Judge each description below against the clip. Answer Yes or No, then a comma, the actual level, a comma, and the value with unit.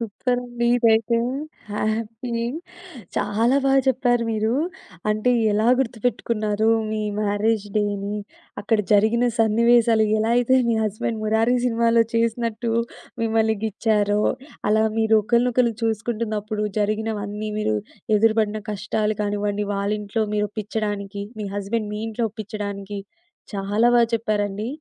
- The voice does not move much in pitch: Yes, narrow, 1.8 semitones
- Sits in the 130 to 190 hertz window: No, high, 220 Hz